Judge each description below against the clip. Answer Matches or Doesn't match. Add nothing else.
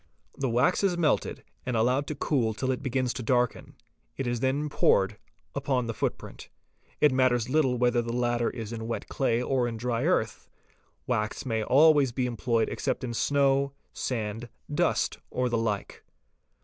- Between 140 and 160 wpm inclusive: Doesn't match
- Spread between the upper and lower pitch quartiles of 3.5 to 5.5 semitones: Doesn't match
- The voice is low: Matches